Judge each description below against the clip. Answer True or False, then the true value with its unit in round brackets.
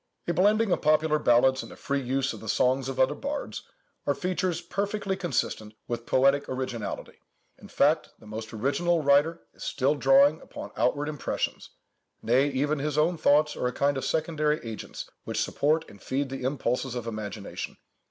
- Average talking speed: True (170 wpm)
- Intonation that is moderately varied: True (3.8 semitones)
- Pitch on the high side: False (140 Hz)